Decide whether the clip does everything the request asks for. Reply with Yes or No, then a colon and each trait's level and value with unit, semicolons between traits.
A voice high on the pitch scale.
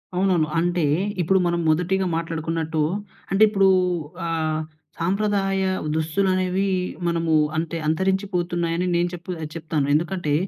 No: medium, 175 Hz